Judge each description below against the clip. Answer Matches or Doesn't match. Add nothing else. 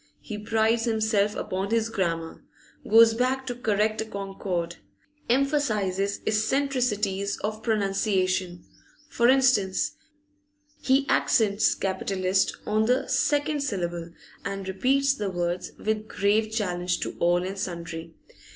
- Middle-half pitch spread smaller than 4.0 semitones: Matches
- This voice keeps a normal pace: Doesn't match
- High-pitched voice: Matches